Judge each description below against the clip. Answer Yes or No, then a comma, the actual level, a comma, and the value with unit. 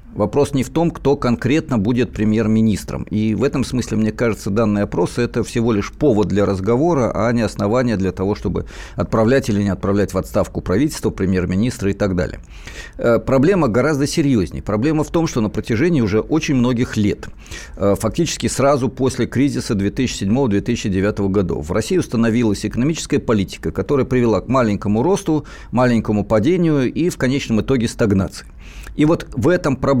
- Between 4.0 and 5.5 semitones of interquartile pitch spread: Yes, average, 4.7 semitones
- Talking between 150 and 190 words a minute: Yes, fast, 160 wpm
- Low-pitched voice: Yes, low, 115 Hz